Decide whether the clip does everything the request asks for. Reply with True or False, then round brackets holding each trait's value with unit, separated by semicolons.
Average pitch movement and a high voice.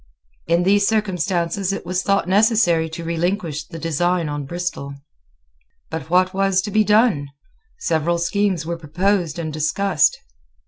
False (3.5 semitones; 175 Hz)